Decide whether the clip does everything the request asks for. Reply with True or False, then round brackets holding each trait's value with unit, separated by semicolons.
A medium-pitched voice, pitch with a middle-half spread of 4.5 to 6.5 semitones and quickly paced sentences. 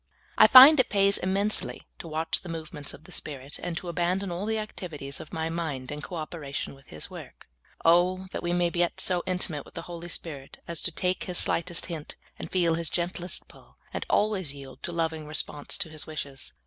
False (170 Hz; 2.9 semitones; 210 wpm)